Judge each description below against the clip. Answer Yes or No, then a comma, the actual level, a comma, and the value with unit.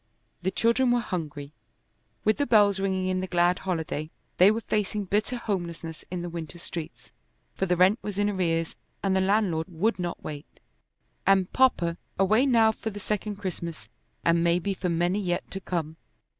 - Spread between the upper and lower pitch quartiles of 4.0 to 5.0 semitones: No, average, 3.4 semitones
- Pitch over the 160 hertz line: Yes, medium, 185 Hz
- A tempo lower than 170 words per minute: No, average, 175 wpm